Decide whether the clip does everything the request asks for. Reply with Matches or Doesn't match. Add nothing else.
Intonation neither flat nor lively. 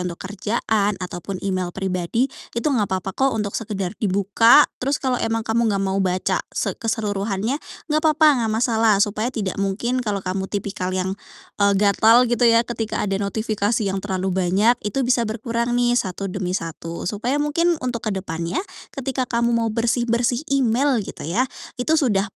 Matches